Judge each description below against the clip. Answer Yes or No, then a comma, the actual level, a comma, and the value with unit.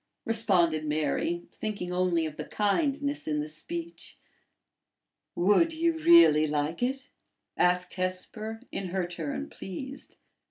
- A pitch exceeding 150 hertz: Yes, medium, 185 Hz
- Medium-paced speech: No, slow, 120 wpm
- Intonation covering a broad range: Yes, wide, 8.3 semitones